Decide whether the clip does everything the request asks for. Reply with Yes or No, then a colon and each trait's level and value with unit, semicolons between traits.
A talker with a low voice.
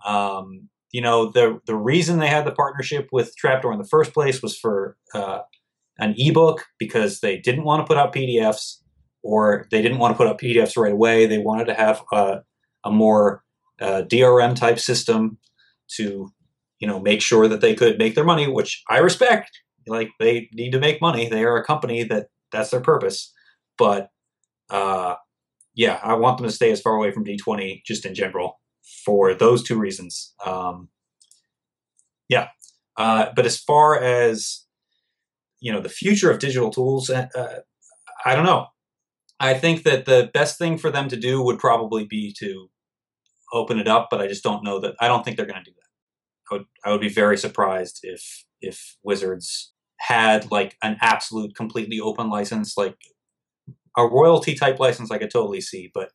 Yes: low, 115 Hz